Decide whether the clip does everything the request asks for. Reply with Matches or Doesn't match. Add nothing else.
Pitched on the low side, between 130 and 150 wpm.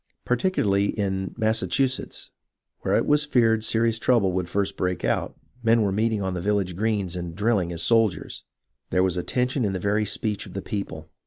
Doesn't match